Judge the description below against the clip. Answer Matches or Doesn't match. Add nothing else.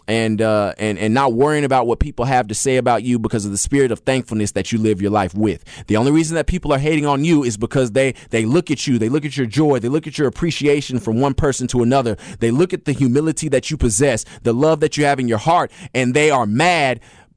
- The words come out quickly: Matches